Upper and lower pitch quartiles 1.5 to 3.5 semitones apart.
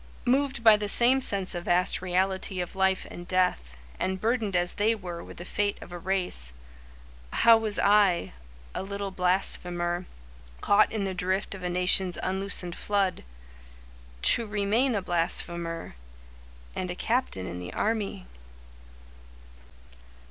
Yes: average, 2.7 semitones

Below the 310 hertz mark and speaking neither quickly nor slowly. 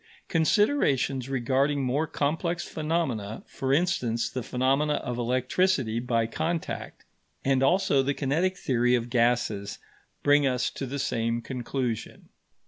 No: low, 135 Hz; slow, 125 wpm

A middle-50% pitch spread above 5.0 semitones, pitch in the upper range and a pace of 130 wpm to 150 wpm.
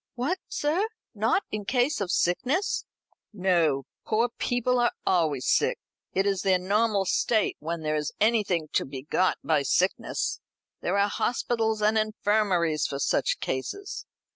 Yes: wide, 5.4 semitones; high, 200 Hz; average, 145 wpm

